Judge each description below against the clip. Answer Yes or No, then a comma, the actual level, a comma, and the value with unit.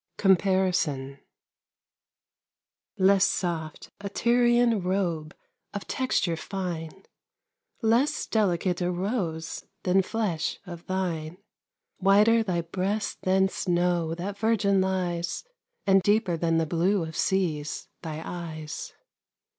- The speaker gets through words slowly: Yes, slow, 105 wpm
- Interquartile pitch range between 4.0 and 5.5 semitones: No, average, 3.1 semitones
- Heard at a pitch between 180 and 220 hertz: Yes, medium, 185 Hz